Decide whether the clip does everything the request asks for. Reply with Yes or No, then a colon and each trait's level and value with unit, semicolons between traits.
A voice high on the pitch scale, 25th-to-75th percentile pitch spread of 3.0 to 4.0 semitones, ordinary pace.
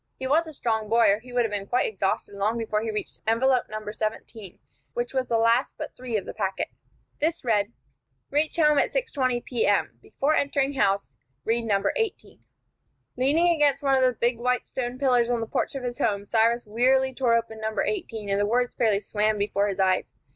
No: high, 235 Hz; average, 3.6 semitones; fast, 210 wpm